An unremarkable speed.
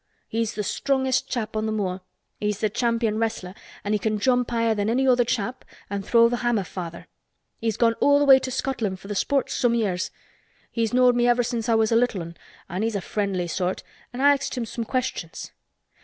No: fast, 215 wpm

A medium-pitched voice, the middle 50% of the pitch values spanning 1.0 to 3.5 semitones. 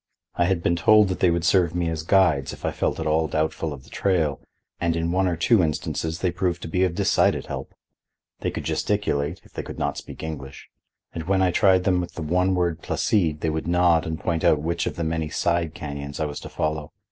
No: very low, 85 Hz; narrow, 2.4 semitones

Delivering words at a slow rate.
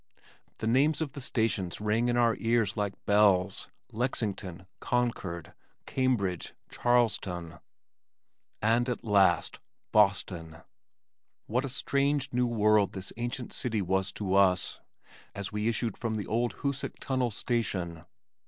Yes: slow, 125 wpm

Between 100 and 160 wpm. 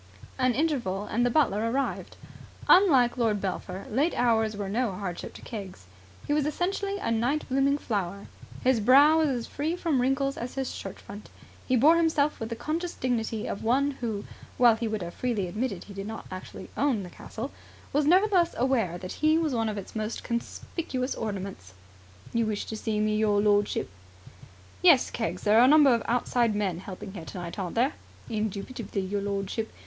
No: average, 185 wpm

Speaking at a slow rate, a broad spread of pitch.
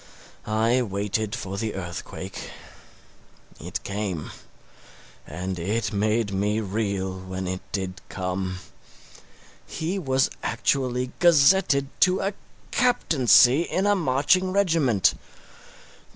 Yes: slow, 100 wpm; wide, 6.6 semitones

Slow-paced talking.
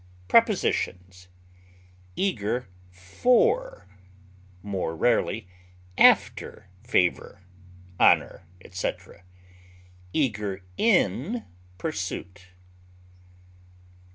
Yes: slow, 50 wpm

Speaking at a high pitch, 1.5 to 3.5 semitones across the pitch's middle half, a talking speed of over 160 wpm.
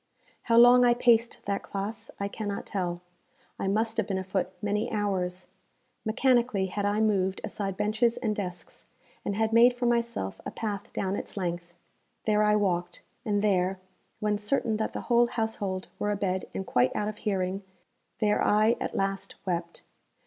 Yes: high, 205 Hz; average, 2.7 semitones; average, 170 wpm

